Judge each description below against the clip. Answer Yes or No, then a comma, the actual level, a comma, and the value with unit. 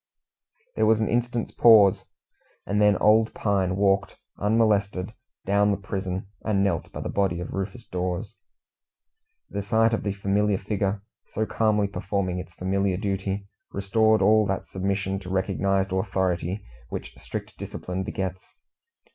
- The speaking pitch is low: Yes, low, 100 Hz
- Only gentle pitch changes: Yes, narrow, 1.8 semitones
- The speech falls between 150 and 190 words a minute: No, average, 140 wpm